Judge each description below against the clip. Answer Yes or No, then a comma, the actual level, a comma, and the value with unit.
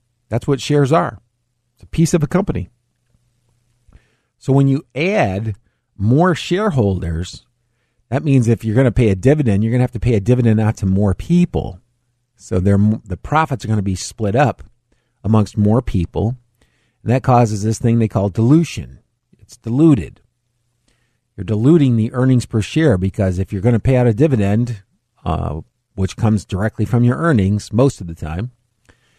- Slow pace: No, average, 175 wpm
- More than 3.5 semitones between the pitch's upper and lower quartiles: No, average, 3.1 semitones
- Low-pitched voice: Yes, low, 120 Hz